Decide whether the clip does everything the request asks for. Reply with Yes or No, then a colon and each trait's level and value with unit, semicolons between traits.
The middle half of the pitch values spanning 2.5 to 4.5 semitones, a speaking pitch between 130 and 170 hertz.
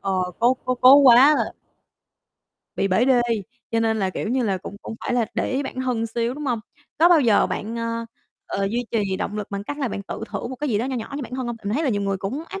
No: average, 3.9 semitones; high, 230 Hz